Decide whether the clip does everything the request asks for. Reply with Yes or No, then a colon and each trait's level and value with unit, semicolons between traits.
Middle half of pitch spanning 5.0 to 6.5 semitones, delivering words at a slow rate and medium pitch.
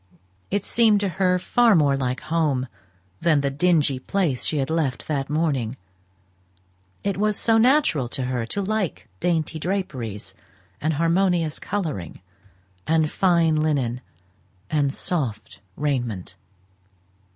Yes: wide, 5.4 semitones; slow, 125 wpm; medium, 155 Hz